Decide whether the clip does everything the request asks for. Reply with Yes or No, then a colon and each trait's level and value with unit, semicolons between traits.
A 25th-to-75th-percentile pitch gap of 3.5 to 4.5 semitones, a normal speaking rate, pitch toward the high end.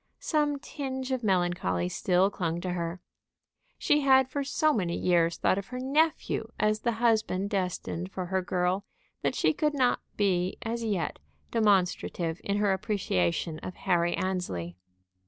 No: average, 5.2 semitones; average, 155 wpm; high, 195 Hz